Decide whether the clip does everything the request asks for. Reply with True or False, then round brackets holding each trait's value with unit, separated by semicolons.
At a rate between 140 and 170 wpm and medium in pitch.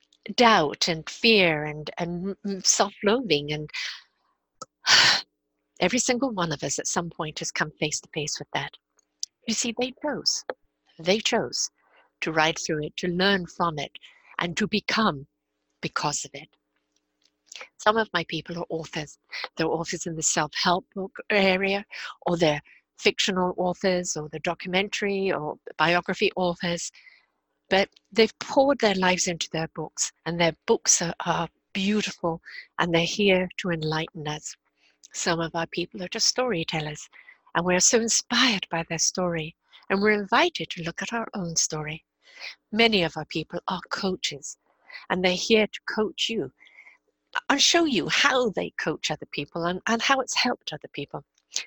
True (155 wpm; 180 Hz)